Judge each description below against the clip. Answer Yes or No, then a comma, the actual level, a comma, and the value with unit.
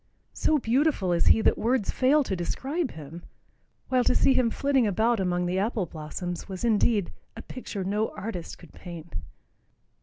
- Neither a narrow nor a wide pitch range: No, wide, 6.1 semitones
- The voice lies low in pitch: No, high, 210 Hz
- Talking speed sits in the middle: Yes, average, 170 wpm